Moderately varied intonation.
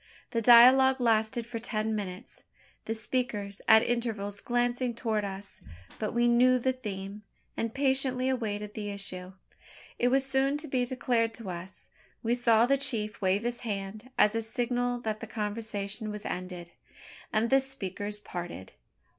Yes: average, 3.1 semitones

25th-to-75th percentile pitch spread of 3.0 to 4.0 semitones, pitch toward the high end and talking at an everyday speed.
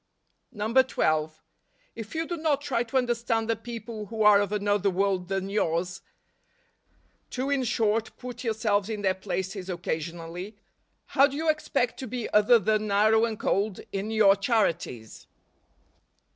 Yes: average, 3.5 semitones; high, 215 Hz; average, 170 wpm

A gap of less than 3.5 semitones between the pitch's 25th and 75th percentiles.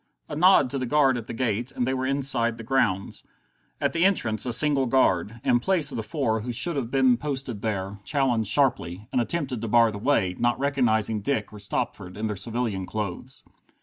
No: average, 4.0 semitones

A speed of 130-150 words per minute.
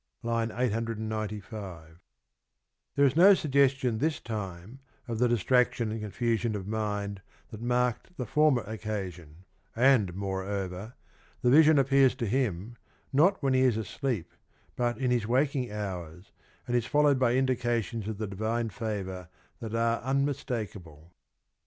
Yes: slow, 135 wpm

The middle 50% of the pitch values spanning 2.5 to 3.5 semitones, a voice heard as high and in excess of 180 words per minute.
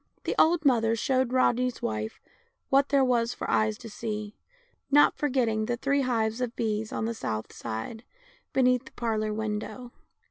No: average, 2.9 semitones; high, 230 Hz; average, 165 wpm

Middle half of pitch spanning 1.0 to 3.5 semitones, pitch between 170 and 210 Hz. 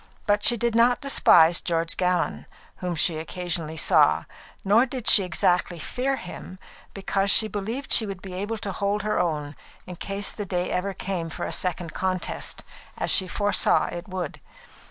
Yes: average, 3.0 semitones; high, 190 Hz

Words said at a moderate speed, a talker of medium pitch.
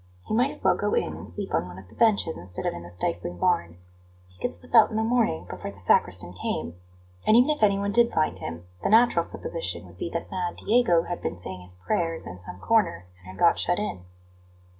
No: fast, 235 wpm; medium, 165 Hz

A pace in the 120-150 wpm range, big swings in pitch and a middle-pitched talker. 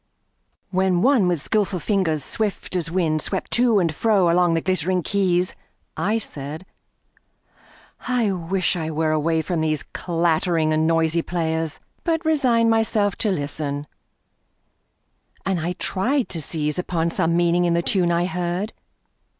No: average, 145 wpm; average, 3.3 semitones; medium, 175 Hz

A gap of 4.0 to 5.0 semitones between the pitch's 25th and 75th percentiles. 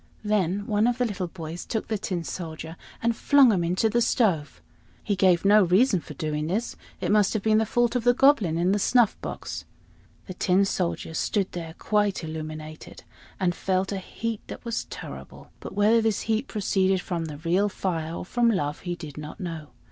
Yes: average, 4.6 semitones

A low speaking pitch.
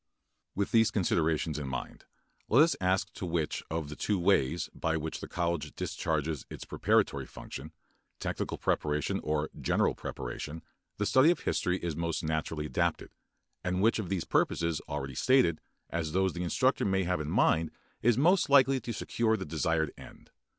Yes: very low, 85 Hz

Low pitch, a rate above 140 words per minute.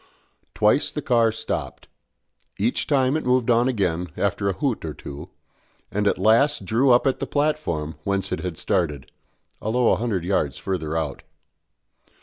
Yes: low, 105 Hz; average, 160 wpm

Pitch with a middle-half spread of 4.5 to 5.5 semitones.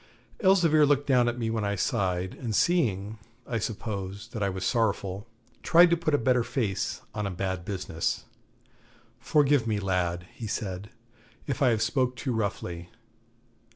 Yes: average, 5.0 semitones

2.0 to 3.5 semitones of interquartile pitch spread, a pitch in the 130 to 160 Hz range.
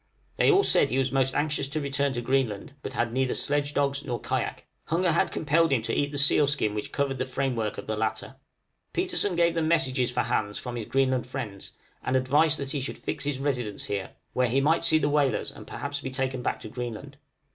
Yes: average, 2.8 semitones; low, 135 Hz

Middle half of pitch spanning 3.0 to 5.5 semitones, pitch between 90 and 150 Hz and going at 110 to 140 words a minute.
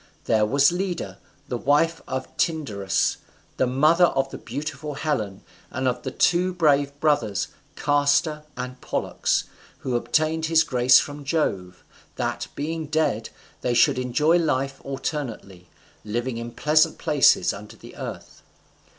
Yes: average, 4.3 semitones; medium, 140 Hz; slow, 135 wpm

